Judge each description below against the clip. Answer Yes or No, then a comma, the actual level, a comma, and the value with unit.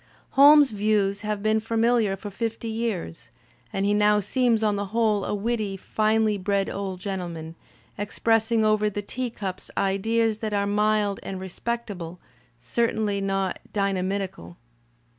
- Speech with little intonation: Yes, narrow, 2.3 semitones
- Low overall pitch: No, high, 210 Hz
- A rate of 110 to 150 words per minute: Yes, average, 140 wpm